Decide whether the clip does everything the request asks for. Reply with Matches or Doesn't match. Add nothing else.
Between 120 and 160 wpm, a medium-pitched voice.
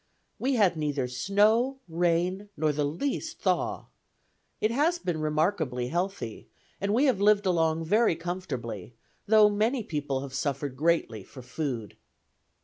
Matches